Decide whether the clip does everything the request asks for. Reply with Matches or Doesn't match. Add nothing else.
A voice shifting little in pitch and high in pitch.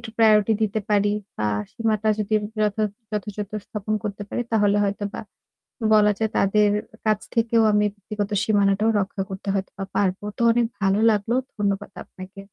Matches